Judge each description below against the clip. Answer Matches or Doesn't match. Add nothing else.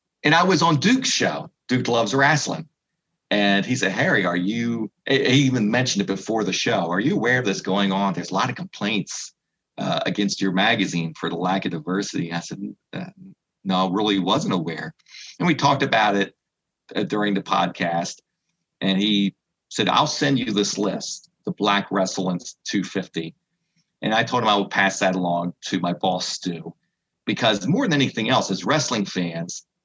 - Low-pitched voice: Matches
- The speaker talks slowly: Doesn't match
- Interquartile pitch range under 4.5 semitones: Doesn't match